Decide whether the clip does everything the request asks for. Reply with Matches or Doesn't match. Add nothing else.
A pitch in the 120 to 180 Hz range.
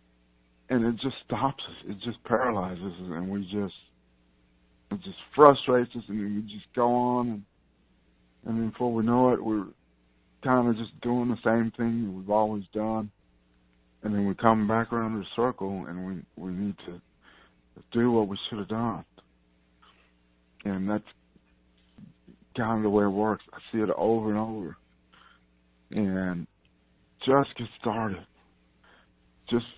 Doesn't match